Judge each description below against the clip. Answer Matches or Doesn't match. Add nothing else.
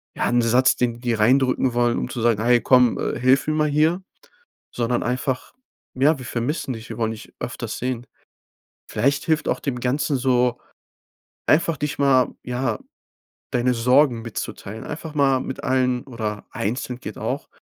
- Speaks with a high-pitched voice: Doesn't match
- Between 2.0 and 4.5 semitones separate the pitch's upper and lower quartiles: Matches